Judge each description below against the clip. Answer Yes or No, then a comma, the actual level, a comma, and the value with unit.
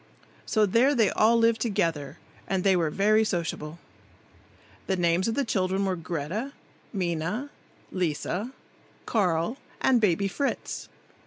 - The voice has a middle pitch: No, high, 195 Hz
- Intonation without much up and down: No, average, 4.7 semitones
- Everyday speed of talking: No, slow, 130 wpm